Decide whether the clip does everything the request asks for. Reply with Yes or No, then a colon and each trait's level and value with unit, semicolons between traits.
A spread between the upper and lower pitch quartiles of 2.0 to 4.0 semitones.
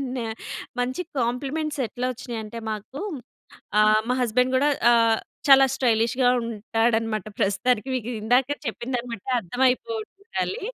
Yes: average, 2.8 semitones